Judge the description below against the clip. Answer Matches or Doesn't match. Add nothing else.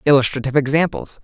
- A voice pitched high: Doesn't match